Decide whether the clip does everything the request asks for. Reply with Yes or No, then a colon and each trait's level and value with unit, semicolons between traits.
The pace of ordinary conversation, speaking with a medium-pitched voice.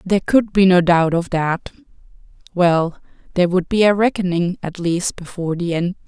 Yes: average, 180 wpm; medium, 180 Hz